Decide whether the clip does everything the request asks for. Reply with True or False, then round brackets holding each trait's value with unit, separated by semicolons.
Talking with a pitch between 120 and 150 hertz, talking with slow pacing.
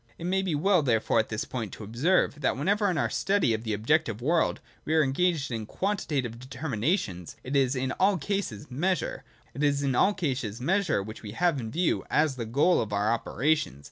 False (140 Hz; 180 wpm)